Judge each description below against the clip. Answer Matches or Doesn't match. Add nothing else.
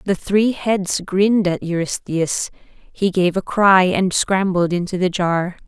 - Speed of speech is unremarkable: Matches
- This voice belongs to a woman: Matches